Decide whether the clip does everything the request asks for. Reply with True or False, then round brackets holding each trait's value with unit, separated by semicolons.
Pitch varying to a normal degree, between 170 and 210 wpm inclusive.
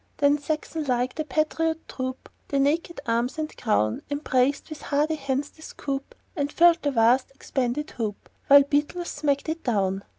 False (3.3 semitones; 160 wpm)